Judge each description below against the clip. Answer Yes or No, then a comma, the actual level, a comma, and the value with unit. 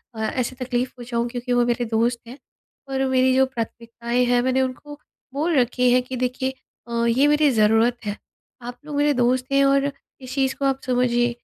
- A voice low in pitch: No, very high, 250 Hz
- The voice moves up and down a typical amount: No, narrow, 1.7 semitones